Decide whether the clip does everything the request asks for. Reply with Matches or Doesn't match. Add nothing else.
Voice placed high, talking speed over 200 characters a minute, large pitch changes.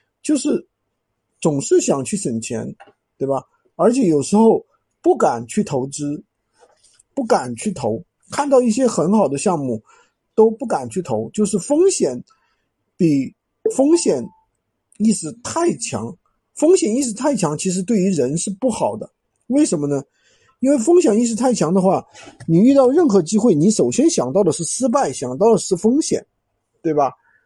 Matches